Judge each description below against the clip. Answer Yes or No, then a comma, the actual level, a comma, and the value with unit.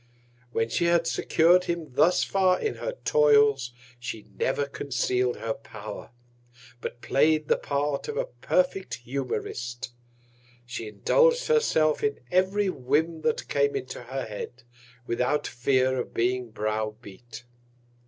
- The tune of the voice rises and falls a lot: Yes, wide, 6.0 semitones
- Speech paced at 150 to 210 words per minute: No, slow, 135 wpm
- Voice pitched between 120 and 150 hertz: Yes, medium, 140 Hz